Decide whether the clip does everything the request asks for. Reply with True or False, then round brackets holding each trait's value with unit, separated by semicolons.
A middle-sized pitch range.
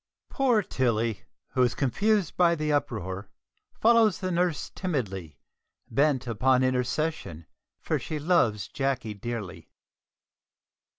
False (7.2 semitones)